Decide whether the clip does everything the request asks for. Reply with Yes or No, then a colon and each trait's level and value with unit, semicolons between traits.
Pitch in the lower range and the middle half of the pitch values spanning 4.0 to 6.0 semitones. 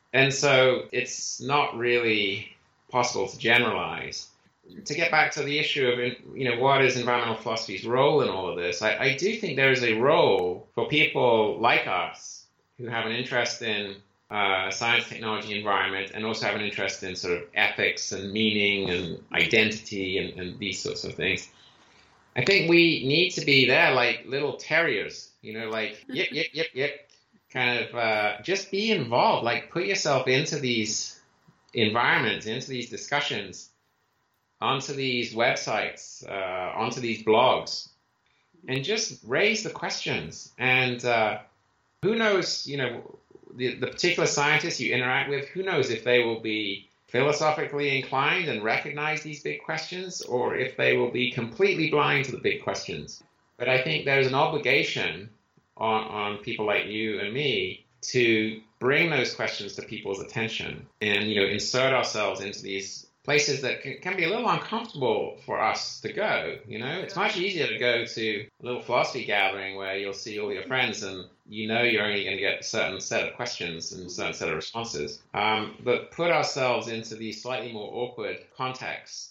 Yes: low, 120 Hz; average, 4.8 semitones